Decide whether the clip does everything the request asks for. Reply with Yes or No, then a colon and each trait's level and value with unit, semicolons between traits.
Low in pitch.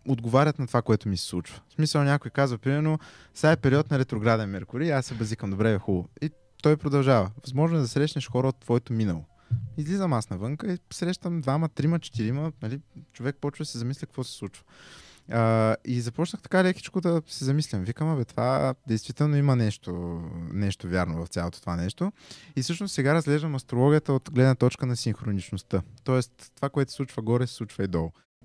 Yes: low, 130 Hz